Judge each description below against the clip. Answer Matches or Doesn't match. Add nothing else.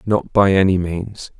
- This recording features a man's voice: Matches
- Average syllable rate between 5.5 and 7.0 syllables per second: Doesn't match